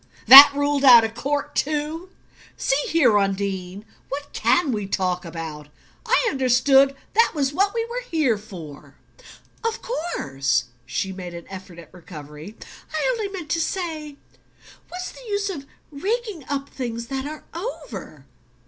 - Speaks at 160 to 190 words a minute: No, average, 150 wpm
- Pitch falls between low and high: No, very high, 275 Hz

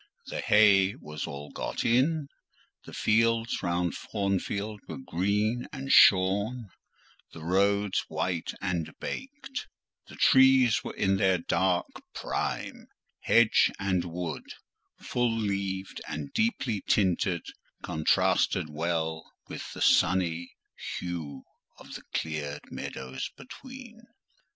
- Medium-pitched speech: No, very low, 95 Hz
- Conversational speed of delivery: No, slow, 110 wpm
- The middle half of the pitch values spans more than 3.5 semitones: Yes, average, 5.2 semitones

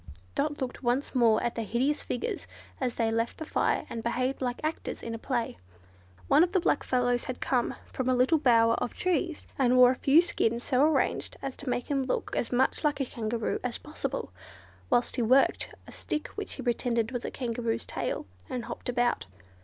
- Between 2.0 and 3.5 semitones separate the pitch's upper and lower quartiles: Yes, narrow, 2.6 semitones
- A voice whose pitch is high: Yes, very high, 250 Hz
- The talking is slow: No, fast, 205 wpm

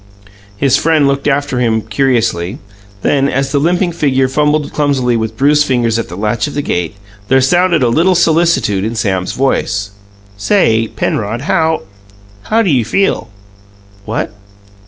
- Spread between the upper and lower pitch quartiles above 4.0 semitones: Yes, average, 5.1 semitones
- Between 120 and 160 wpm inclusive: Yes, average, 155 wpm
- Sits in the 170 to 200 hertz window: No, low, 135 Hz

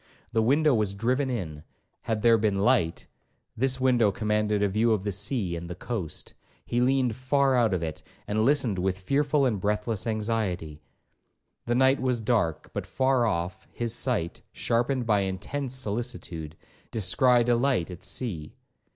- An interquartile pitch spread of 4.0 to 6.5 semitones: Yes, average, 4.6 semitones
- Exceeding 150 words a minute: Yes, average, 160 wpm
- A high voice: No, low, 110 Hz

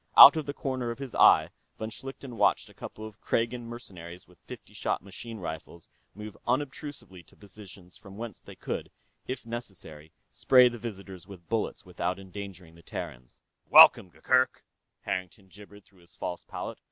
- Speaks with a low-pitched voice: Yes, low, 100 Hz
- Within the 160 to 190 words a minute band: Yes, average, 165 wpm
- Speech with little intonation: No, average, 4.7 semitones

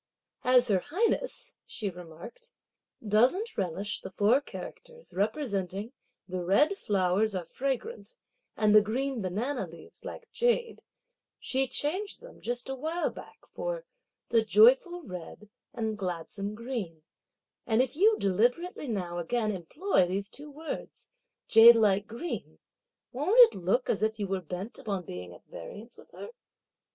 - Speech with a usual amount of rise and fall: No, wide, 7.4 semitones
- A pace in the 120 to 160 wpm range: Yes, average, 145 wpm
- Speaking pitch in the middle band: No, high, 225 Hz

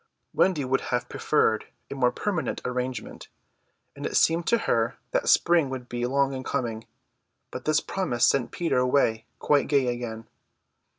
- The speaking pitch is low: Yes, low, 130 Hz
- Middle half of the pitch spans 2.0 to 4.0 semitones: Yes, average, 3.6 semitones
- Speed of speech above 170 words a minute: No, average, 160 wpm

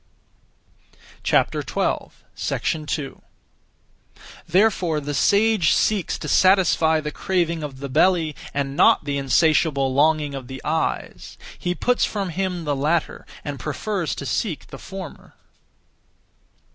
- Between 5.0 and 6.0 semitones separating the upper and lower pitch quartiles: No, average, 4.5 semitones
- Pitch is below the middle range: No, medium, 160 Hz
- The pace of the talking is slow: Yes, slow, 115 wpm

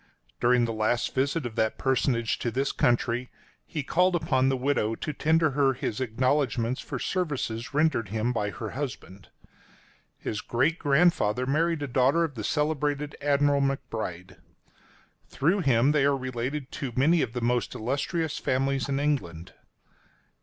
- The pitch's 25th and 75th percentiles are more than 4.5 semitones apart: No, average, 3.7 semitones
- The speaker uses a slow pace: No, average, 155 wpm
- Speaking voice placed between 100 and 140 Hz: Yes, low, 135 Hz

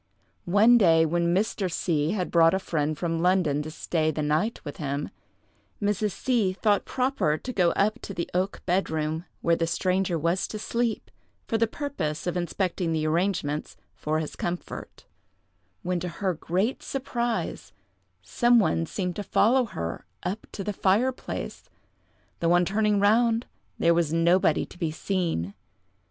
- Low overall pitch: No, medium, 180 Hz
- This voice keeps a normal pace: Yes, average, 160 wpm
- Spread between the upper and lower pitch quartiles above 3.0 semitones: Yes, average, 4.2 semitones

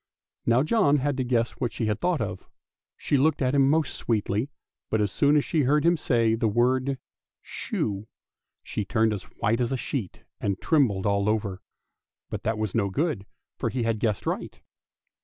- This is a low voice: Yes, low, 115 Hz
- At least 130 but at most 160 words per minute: No, average, 190 wpm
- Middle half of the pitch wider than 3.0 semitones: Yes, average, 4.8 semitones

